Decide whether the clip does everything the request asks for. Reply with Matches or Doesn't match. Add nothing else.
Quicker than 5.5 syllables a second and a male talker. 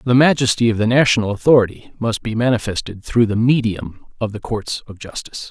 Matches